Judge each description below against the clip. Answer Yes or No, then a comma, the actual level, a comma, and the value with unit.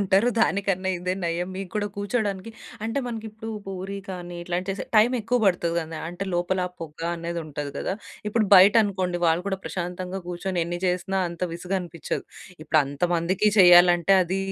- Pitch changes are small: Yes, narrow, 2.2 semitones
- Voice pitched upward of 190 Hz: No, medium, 185 Hz